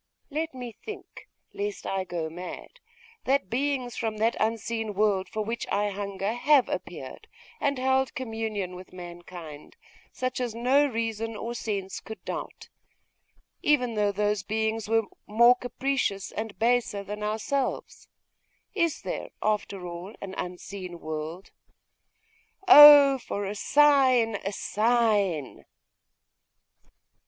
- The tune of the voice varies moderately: Yes, average, 4.2 semitones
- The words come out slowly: Yes, slow, 125 wpm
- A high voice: Yes, high, 220 Hz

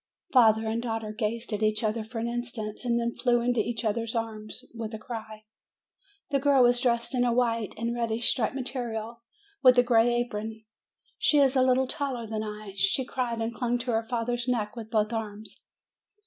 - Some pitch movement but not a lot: No, narrow, 1.9 semitones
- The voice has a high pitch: Yes, high, 235 Hz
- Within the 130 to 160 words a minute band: No, average, 190 wpm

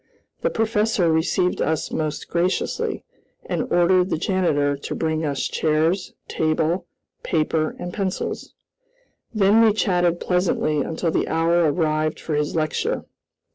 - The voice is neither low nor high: Yes, medium, 165 Hz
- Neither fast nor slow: No, slow, 130 wpm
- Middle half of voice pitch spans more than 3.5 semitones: No, average, 2.8 semitones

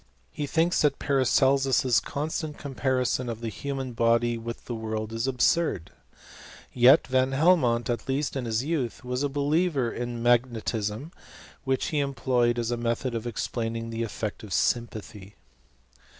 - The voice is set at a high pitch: No, low, 125 Hz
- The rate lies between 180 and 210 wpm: No, average, 150 wpm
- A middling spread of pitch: Yes, average, 3.0 semitones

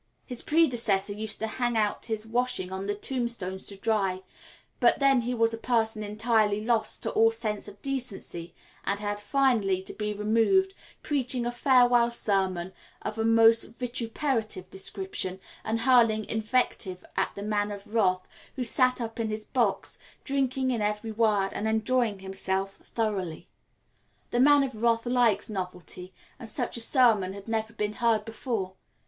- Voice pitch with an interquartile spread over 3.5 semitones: No, average, 3.0 semitones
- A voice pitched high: Yes, high, 220 Hz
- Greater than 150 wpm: Yes, average, 160 wpm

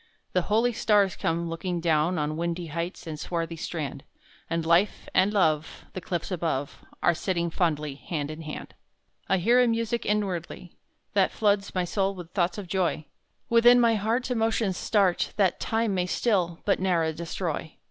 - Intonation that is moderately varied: Yes, average, 3.9 semitones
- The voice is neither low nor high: Yes, medium, 180 Hz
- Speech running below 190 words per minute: Yes, average, 170 wpm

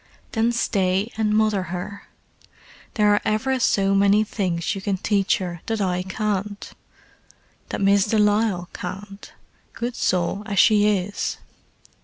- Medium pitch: No, high, 200 Hz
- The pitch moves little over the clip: Yes, narrow, 2.1 semitones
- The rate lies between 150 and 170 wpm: No, average, 140 wpm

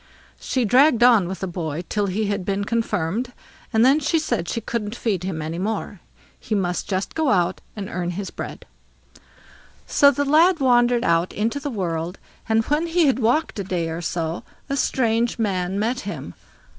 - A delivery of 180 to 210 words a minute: Yes, average, 190 wpm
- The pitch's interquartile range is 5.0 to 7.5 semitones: Yes, wide, 5.5 semitones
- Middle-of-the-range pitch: No, high, 210 Hz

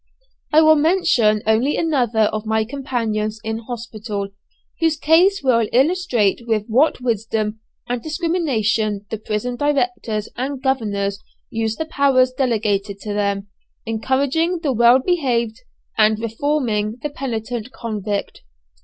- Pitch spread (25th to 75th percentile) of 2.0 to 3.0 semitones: No, average, 4.4 semitones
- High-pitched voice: Yes, high, 235 Hz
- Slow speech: Yes, slow, 125 wpm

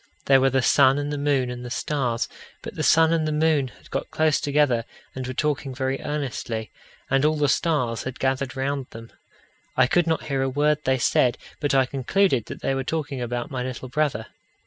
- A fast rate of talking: Yes, fast, 215 wpm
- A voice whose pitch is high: No, low, 135 Hz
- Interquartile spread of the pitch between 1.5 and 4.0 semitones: Yes, average, 2.7 semitones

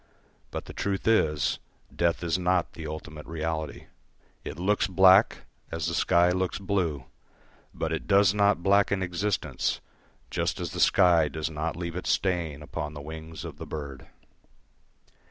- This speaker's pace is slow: No, average, 155 wpm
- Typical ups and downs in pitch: Yes, average, 3.1 semitones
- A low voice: Yes, very low, 85 Hz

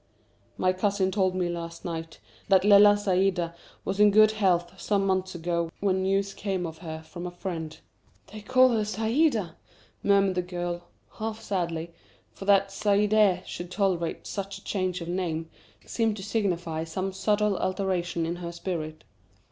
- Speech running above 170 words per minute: No, average, 160 wpm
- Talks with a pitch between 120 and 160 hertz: No, medium, 185 Hz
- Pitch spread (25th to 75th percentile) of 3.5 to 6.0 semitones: No, average, 2.8 semitones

